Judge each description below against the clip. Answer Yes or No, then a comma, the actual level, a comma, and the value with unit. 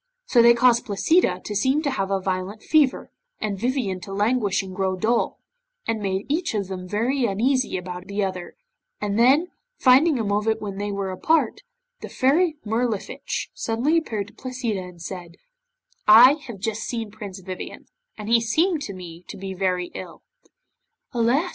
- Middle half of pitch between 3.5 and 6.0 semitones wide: Yes, average, 4.7 semitones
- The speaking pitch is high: Yes, high, 215 Hz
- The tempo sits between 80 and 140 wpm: No, average, 175 wpm